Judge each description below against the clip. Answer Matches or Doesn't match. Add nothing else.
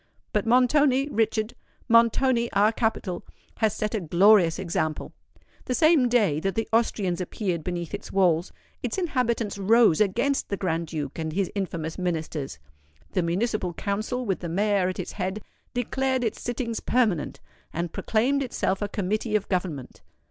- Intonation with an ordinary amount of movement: Matches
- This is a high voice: Matches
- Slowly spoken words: Doesn't match